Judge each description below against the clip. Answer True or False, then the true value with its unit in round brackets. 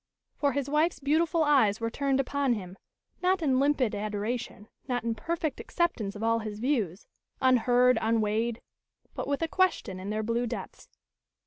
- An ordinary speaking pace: True (160 wpm)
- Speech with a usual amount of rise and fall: True (4.6 semitones)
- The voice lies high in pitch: True (245 Hz)